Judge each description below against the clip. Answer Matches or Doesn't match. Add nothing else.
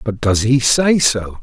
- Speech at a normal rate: Doesn't match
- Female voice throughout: Doesn't match